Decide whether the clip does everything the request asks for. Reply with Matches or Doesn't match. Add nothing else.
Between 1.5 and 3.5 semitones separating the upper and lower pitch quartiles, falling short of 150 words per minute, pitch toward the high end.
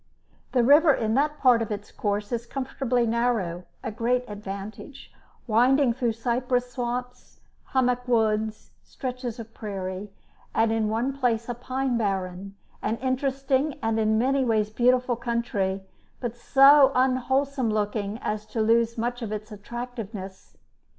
Matches